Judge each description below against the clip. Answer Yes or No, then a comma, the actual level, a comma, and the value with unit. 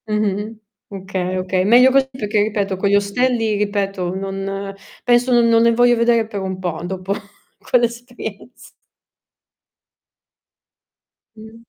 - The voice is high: Yes, high, 210 Hz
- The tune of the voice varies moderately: Yes, average, 3.2 semitones